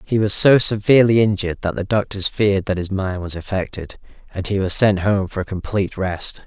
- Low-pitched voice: Yes, low, 100 Hz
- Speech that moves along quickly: Yes, fast, 215 wpm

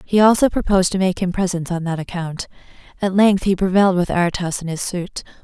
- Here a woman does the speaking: Yes, female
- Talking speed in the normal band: No, fast, 210 wpm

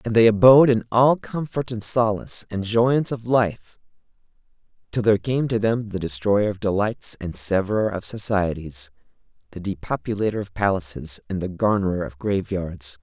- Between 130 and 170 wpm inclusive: Yes, average, 155 wpm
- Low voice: Yes, low, 105 Hz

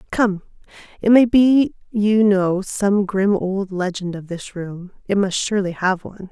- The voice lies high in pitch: Yes, high, 195 Hz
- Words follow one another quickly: No, average, 160 wpm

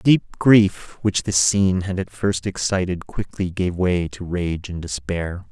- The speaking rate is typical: Yes, average, 185 wpm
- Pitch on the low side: Yes, very low, 90 Hz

